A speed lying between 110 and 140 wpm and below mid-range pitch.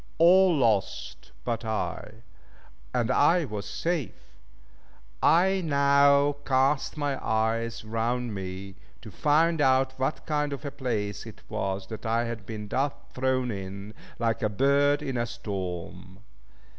Yes: slow, 135 wpm; low, 120 Hz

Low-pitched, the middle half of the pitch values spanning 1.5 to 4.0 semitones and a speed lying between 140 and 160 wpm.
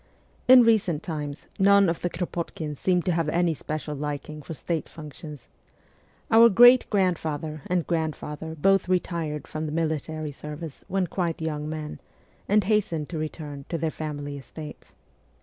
No: medium, 160 Hz; average, 3.0 semitones; average, 155 wpm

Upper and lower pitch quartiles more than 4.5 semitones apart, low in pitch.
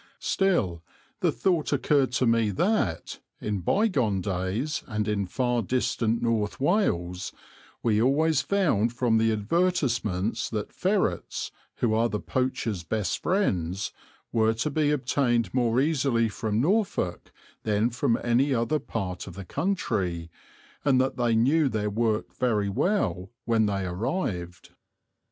Yes: average, 5.2 semitones; low, 115 Hz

